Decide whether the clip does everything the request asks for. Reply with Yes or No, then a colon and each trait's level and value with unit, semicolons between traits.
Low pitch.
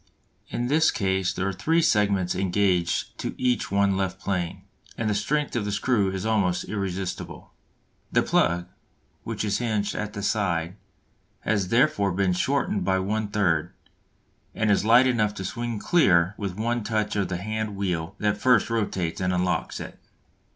Yes: low, 100 Hz